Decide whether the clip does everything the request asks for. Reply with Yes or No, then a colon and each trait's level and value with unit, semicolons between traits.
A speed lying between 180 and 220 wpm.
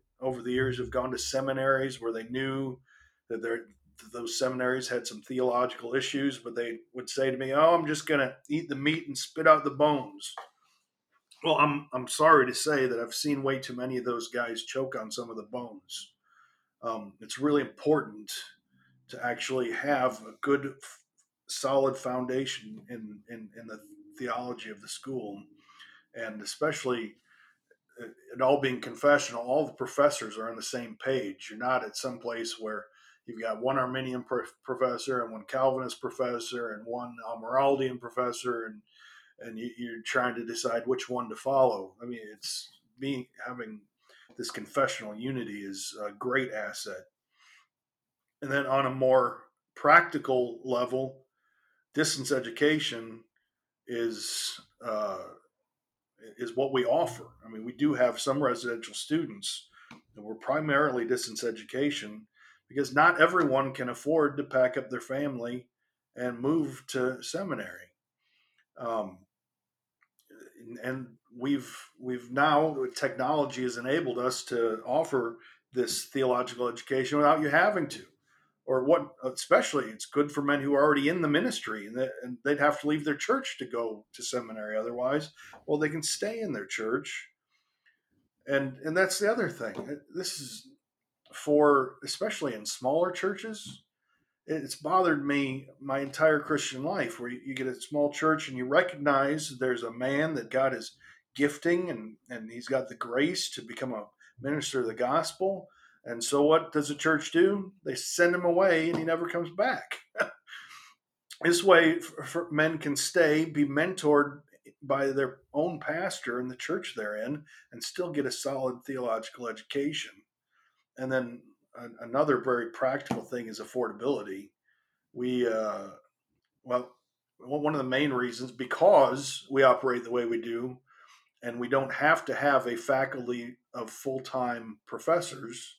No: average, 155 wpm